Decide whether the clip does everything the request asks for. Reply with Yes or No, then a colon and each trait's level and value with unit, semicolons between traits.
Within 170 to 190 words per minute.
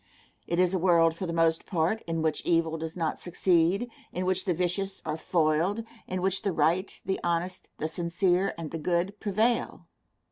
Yes: average, 185 wpm